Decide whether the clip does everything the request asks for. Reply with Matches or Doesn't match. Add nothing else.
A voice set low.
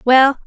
Doesn't match